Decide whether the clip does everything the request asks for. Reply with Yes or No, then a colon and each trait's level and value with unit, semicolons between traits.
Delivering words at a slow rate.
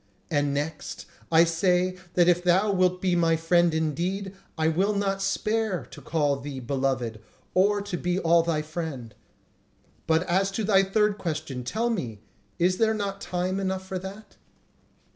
No: average, 160 wpm